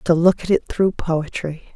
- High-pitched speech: No, medium, 170 Hz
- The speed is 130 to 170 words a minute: No, fast, 205 wpm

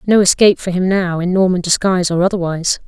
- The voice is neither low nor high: Yes, medium, 180 Hz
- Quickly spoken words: Yes, fast, 210 wpm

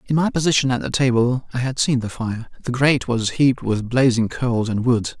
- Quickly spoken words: Yes, fast, 230 wpm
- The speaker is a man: Yes, male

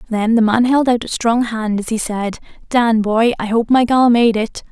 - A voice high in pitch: Yes, high, 230 Hz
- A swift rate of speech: Yes, fast, 240 wpm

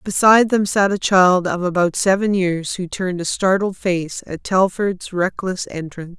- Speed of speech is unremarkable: Yes, average, 175 wpm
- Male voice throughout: No, female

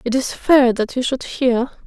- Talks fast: Yes, fast, 225 wpm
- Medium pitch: No, very high, 250 Hz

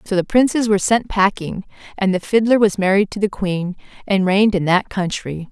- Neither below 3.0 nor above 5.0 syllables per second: No, 5.4 syllables/s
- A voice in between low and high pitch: No, high, 195 Hz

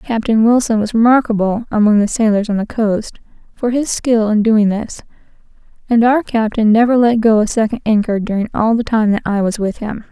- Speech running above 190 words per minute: Yes, average, 200 wpm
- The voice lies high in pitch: Yes, high, 220 Hz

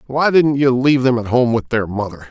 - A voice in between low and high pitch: No, low, 125 Hz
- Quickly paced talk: Yes, fast, 260 wpm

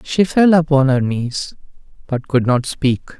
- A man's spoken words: Yes, male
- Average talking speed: Yes, average, 170 wpm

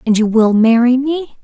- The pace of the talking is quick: Yes, fast, 210 wpm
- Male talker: No, female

